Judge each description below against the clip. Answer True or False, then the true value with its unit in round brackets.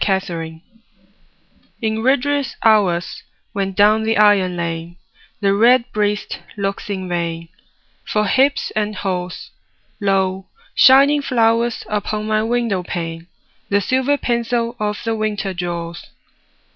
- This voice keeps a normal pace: False (115 wpm)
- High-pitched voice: True (210 Hz)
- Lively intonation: False (3.9 semitones)